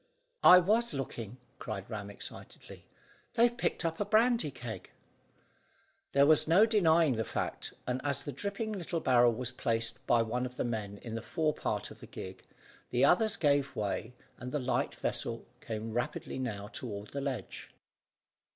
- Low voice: Yes, low, 130 Hz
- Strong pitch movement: Yes, wide, 6.5 semitones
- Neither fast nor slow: Yes, average, 170 wpm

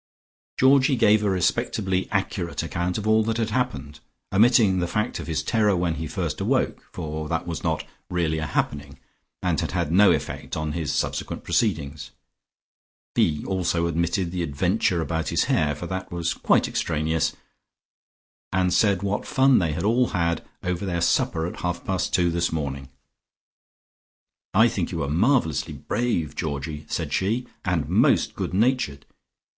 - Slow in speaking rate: No, average, 160 wpm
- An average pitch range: Yes, average, 4.4 semitones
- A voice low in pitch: Yes, very low, 85 Hz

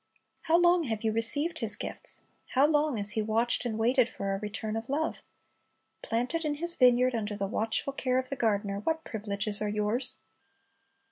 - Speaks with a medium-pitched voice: No, high, 230 Hz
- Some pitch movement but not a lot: Yes, average, 4.8 semitones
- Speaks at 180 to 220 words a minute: Yes, average, 185 wpm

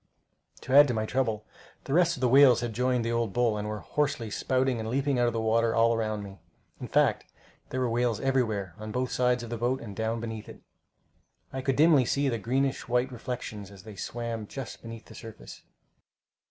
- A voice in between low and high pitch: No, low, 120 Hz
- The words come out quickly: Yes, fast, 215 wpm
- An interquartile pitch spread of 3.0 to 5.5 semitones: No, narrow, 2.6 semitones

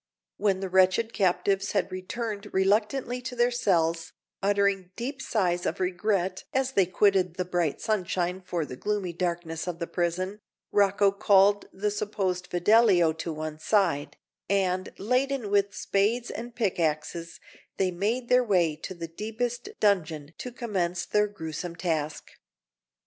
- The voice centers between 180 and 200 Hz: Yes, high, 190 Hz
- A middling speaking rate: Yes, average, 145 wpm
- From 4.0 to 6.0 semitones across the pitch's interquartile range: No, average, 3.2 semitones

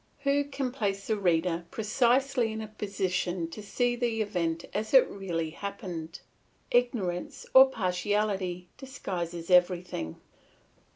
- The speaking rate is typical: No, slow, 120 wpm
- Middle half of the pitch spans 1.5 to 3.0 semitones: No, average, 5.1 semitones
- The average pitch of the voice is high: Yes, high, 200 Hz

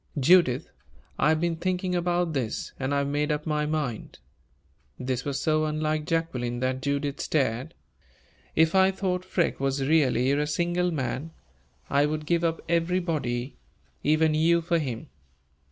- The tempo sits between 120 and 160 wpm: Yes, average, 155 wpm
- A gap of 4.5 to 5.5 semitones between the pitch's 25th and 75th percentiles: No, average, 3.6 semitones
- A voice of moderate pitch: Yes, medium, 155 Hz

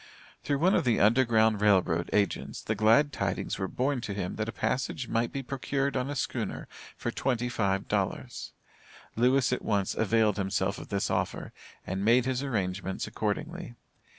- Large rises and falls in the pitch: No, average, 4.6 semitones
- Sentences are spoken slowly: No, average, 175 wpm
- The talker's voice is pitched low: Yes, low, 115 Hz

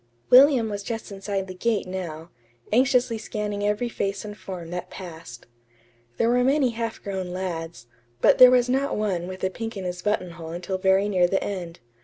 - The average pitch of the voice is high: Yes, high, 195 Hz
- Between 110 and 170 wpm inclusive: No, average, 185 wpm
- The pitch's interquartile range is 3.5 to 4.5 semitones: Yes, average, 4.1 semitones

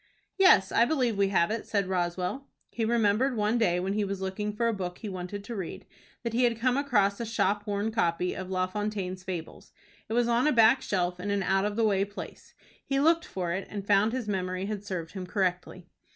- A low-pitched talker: No, high, 205 Hz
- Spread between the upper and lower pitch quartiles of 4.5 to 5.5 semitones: No, average, 3.5 semitones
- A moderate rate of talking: No, fast, 225 wpm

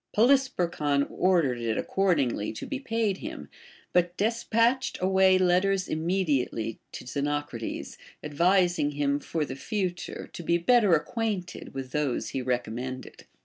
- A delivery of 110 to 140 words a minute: Yes, slow, 135 wpm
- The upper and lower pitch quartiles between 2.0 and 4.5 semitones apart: No, wide, 5.5 semitones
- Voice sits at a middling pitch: Yes, medium, 170 Hz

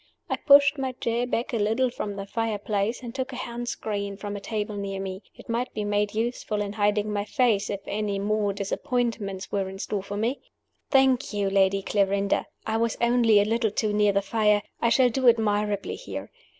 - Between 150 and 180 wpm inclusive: No, fast, 205 wpm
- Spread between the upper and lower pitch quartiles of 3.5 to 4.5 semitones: No, average, 2.7 semitones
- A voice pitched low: No, high, 210 Hz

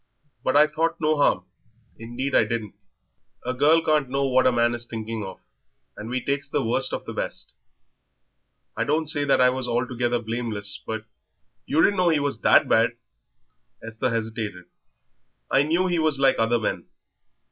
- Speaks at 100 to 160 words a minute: No, average, 180 wpm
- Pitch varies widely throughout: No, average, 4.2 semitones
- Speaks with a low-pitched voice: Yes, low, 125 Hz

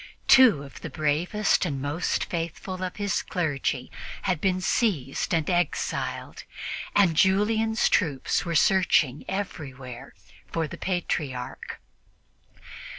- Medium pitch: Yes, medium, 170 Hz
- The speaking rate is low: Yes, slow, 110 wpm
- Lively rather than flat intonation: No, average, 4.9 semitones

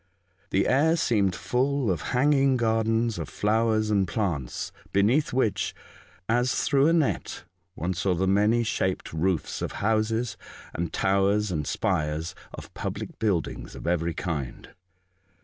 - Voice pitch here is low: Yes, low, 105 Hz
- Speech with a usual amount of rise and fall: Yes, average, 4.6 semitones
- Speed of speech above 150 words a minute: No, slow, 135 wpm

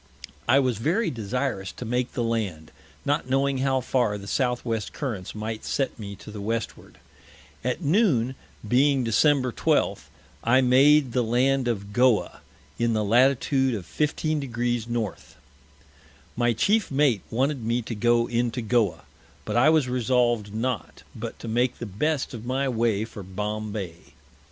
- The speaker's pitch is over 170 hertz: No, low, 120 Hz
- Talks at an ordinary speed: Yes, average, 155 wpm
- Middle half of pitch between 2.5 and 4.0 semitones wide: Yes, average, 3.2 semitones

